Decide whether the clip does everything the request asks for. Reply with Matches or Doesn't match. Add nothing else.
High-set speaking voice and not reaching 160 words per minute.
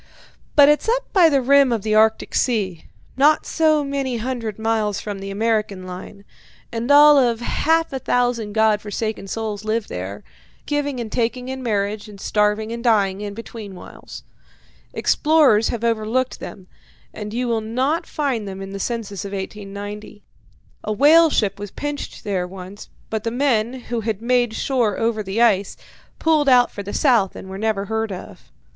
Doesn't match